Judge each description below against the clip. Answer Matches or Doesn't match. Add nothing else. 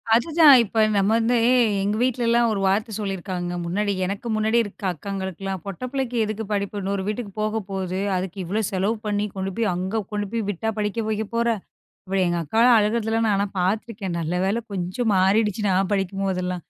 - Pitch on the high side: Matches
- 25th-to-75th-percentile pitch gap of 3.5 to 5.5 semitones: Doesn't match